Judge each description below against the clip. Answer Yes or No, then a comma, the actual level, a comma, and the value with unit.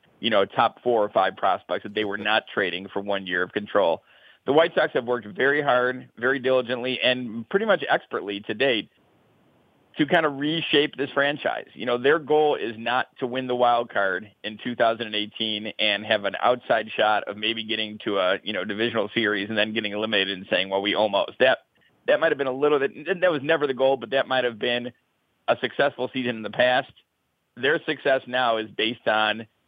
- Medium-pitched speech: No, low, 120 Hz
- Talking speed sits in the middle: No, fast, 210 wpm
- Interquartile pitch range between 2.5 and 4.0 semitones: Yes, average, 3.6 semitones